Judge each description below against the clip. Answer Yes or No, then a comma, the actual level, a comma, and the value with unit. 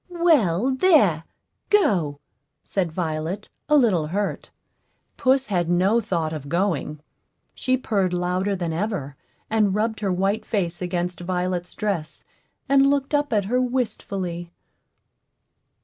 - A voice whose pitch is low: No, high, 195 Hz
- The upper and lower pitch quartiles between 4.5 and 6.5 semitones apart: Yes, average, 5.1 semitones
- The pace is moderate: No, slow, 125 wpm